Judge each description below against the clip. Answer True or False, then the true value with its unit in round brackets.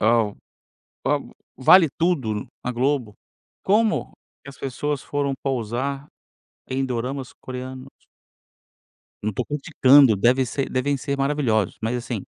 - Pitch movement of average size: True (3.0 semitones)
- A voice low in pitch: True (130 Hz)